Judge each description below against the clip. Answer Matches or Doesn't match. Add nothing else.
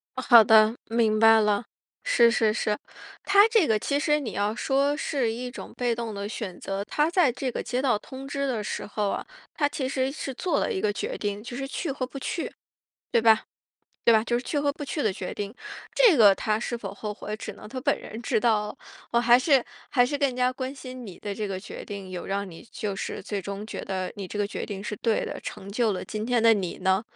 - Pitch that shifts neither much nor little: Matches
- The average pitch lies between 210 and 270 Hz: Matches